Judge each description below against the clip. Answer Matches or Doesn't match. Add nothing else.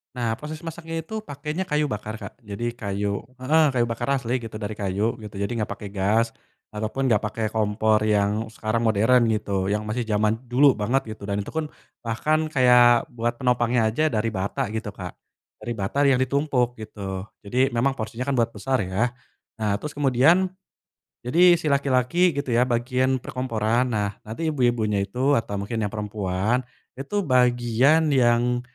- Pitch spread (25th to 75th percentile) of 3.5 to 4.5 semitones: Matches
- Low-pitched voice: Matches